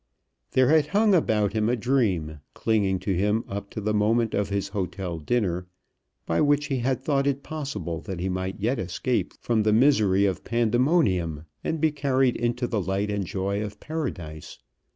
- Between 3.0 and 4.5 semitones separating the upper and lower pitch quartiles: No, wide, 5.4 semitones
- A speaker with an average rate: Yes, average, 180 wpm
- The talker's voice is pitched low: Yes, low, 110 Hz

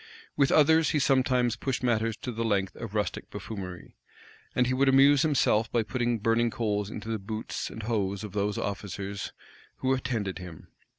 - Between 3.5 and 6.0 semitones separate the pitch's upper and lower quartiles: Yes, average, 3.9 semitones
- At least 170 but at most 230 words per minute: Yes, average, 180 wpm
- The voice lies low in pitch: Yes, low, 115 Hz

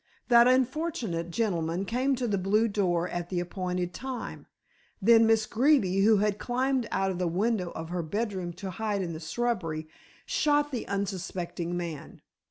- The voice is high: Yes, high, 200 Hz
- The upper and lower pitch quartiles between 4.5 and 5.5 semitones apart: Yes, average, 5.2 semitones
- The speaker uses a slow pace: No, average, 165 wpm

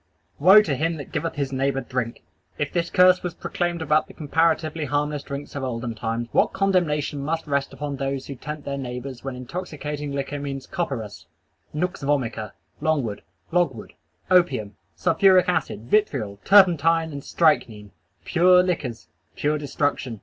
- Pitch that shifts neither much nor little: Yes, average, 3.9 semitones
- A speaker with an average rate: Yes, average, 150 wpm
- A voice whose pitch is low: No, medium, 145 Hz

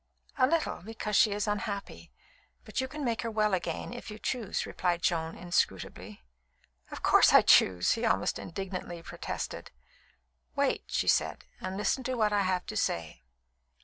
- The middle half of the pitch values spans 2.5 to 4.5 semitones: Yes, average, 4.1 semitones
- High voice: Yes, high, 205 Hz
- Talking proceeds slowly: No, average, 165 wpm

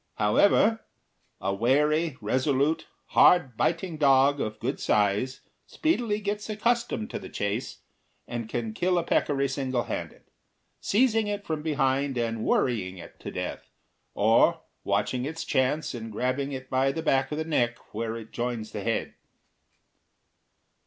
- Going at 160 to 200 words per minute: No, average, 145 wpm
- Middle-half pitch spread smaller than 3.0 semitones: No, wide, 5.6 semitones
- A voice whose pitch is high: No, low, 135 Hz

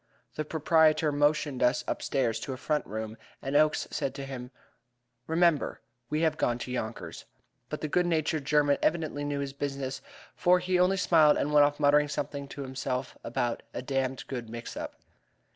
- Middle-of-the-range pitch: Yes, medium, 145 Hz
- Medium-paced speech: Yes, average, 175 wpm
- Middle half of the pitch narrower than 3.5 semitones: Yes, average, 2.7 semitones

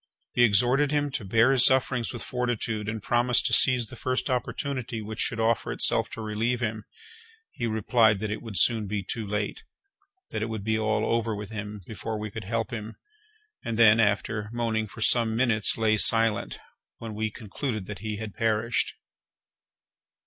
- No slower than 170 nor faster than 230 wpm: Yes, average, 180 wpm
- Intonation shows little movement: Yes, narrow, 1.9 semitones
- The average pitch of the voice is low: Yes, low, 110 Hz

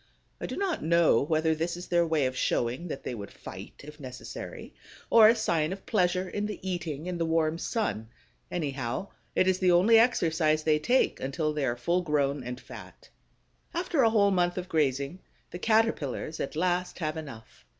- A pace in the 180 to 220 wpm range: Yes, average, 190 wpm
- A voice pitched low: No, medium, 165 Hz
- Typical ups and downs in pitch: Yes, average, 4.0 semitones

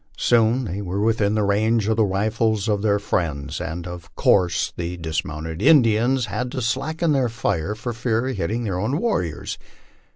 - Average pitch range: Yes, average, 4.7 semitones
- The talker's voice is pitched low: Yes, low, 105 Hz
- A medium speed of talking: Yes, average, 185 wpm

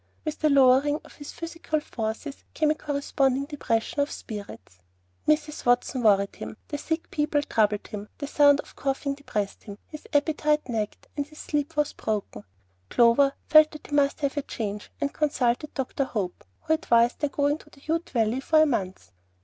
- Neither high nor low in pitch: No, very high, 280 Hz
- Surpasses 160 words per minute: Yes, average, 180 wpm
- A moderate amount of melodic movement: Yes, average, 4.4 semitones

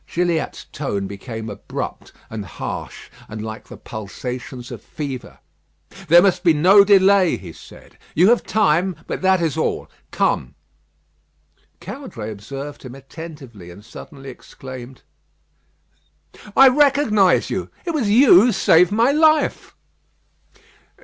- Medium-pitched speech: Yes, medium, 160 Hz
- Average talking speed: No, slow, 125 wpm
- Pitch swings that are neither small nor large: No, wide, 8.6 semitones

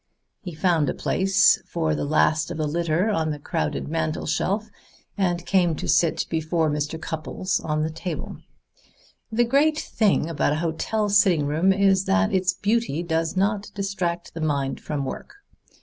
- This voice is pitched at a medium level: Yes, medium, 170 Hz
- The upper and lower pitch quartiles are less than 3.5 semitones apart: No, average, 3.8 semitones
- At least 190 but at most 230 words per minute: No, average, 165 wpm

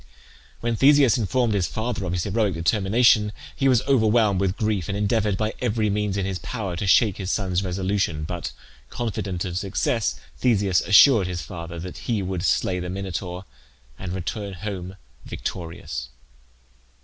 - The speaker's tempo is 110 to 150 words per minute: No, average, 160 wpm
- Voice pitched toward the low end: Yes, low, 100 Hz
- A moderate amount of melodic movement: Yes, average, 3.2 semitones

